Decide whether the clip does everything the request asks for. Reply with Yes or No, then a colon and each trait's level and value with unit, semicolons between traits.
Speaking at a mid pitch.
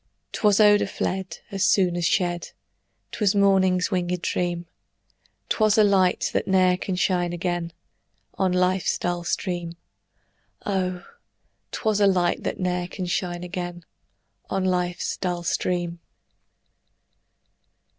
Yes: medium, 180 Hz